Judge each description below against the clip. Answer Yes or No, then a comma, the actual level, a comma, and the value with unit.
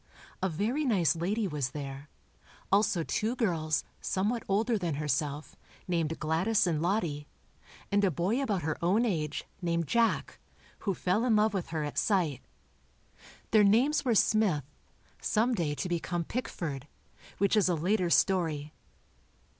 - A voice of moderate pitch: Yes, medium, 180 Hz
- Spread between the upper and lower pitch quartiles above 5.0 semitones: Yes, wide, 5.4 semitones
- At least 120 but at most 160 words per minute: Yes, average, 145 wpm